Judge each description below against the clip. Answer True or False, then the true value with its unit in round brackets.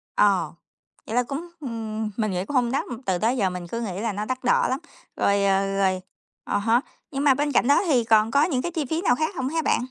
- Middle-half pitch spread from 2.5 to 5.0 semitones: False (5.4 semitones)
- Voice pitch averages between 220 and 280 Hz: True (235 Hz)